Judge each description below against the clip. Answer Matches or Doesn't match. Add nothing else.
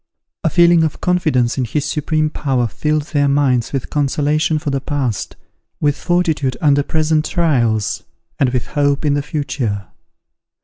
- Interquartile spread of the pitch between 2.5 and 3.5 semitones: Matches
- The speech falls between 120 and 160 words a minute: Matches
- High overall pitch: Doesn't match